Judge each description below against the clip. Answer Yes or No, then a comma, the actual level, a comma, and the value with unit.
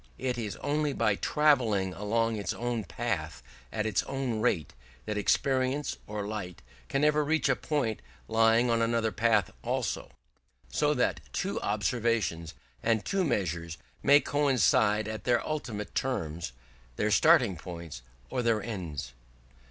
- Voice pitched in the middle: No, low, 110 Hz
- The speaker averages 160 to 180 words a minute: No, average, 140 wpm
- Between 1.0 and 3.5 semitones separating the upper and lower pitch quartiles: No, average, 4.3 semitones